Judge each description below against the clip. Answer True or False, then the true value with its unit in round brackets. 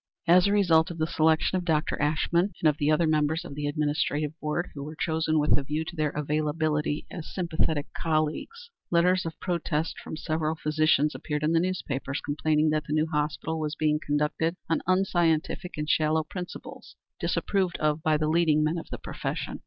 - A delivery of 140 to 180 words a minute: False (190 wpm)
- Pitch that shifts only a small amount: True (1.7 semitones)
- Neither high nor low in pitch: True (155 Hz)